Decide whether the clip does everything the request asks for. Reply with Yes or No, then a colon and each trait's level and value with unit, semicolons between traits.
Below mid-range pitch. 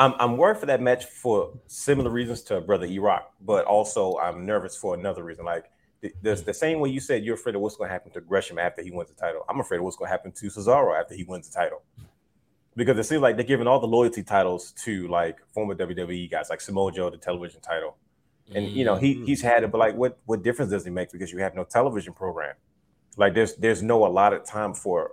Yes: low, 110 Hz